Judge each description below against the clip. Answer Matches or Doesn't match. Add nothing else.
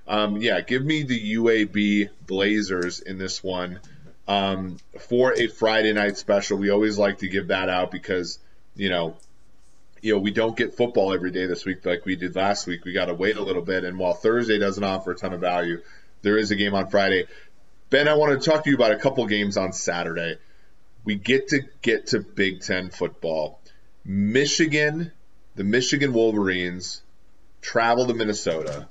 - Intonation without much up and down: Doesn't match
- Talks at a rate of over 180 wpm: Matches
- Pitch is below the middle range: Matches